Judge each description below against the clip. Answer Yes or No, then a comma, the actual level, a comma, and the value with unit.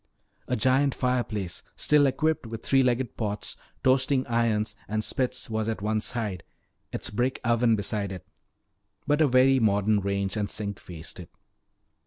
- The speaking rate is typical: Yes, average, 155 wpm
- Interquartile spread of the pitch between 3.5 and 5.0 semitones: Yes, average, 4.0 semitones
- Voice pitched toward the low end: Yes, low, 115 Hz